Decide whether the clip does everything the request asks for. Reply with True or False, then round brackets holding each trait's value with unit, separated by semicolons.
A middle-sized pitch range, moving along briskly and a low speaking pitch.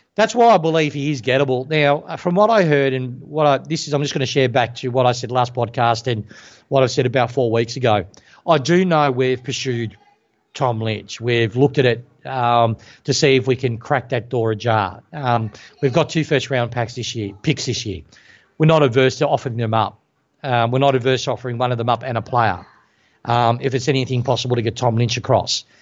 True (3.2 semitones; 230 wpm; 130 Hz)